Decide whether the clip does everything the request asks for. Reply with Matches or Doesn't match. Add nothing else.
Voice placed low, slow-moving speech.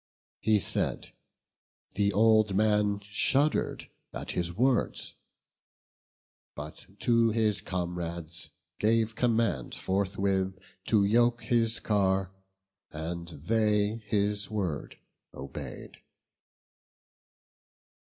Matches